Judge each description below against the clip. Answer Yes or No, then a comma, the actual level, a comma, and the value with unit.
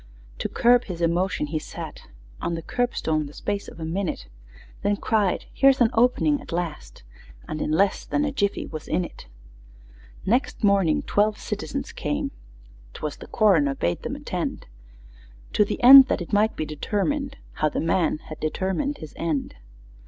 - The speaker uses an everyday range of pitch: No, wide, 6.7 semitones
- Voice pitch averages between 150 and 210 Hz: Yes, high, 190 Hz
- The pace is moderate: Yes, average, 165 wpm